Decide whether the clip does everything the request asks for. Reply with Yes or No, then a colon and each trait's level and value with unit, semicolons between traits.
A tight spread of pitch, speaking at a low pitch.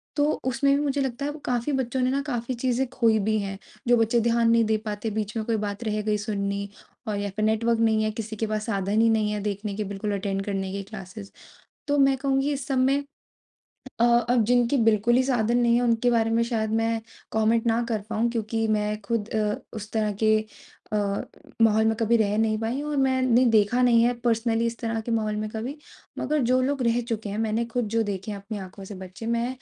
No: narrow, 2.2 semitones; high, 225 Hz